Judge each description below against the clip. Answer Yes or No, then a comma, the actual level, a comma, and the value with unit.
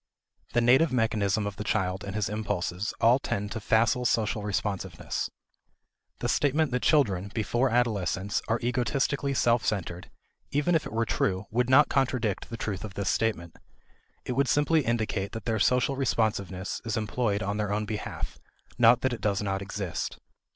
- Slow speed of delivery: No, average, 170 wpm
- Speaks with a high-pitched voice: No, low, 110 Hz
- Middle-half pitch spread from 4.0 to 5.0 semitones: No, average, 3.6 semitones